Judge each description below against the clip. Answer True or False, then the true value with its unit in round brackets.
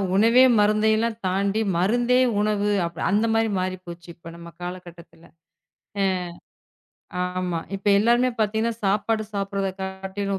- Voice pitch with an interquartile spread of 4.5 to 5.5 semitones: False (3.1 semitones)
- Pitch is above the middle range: True (200 Hz)